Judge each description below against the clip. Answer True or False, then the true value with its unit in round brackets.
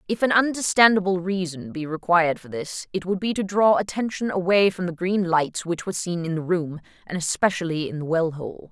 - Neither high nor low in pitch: True (180 Hz)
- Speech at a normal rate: False (215 wpm)